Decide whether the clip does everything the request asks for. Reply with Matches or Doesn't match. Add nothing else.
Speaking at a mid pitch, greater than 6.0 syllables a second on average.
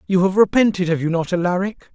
Matches